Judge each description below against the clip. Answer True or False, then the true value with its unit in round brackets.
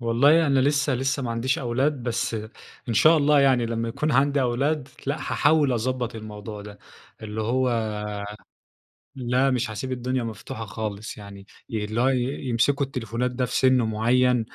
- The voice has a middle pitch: False (125 Hz)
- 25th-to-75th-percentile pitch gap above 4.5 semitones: False (3.2 semitones)